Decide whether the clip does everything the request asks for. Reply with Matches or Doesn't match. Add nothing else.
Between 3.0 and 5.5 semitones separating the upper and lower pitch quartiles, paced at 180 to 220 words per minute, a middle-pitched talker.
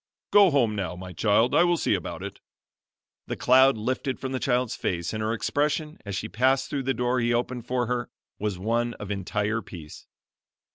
Doesn't match